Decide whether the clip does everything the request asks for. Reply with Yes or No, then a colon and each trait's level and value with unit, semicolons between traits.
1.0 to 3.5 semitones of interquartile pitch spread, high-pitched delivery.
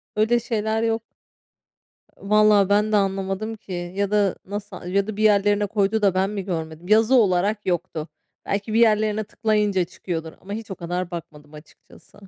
Yes: narrow, 2.6 semitones; high, 200 Hz